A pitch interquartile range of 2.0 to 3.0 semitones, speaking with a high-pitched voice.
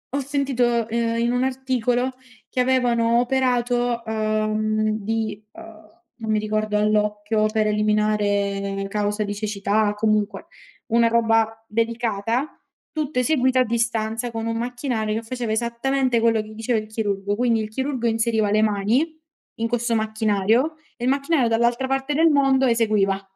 Yes: narrow, 2.4 semitones; high, 225 Hz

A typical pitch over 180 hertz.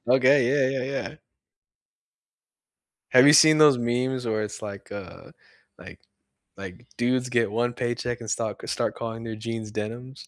No: low, 120 Hz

